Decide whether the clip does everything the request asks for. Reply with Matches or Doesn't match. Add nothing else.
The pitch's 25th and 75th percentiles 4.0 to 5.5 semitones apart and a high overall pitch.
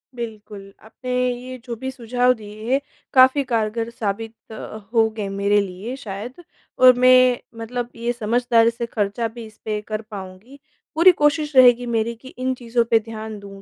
Doesn't match